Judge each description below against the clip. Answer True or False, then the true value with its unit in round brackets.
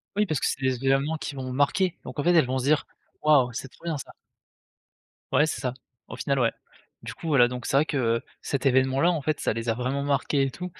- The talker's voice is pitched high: False (135 Hz)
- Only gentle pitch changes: False (3.0 semitones)